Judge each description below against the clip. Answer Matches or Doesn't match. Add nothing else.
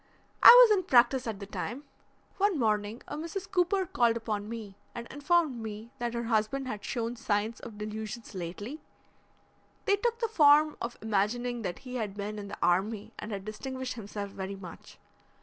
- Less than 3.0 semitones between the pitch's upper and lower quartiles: Doesn't match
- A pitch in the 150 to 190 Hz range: Doesn't match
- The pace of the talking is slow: Doesn't match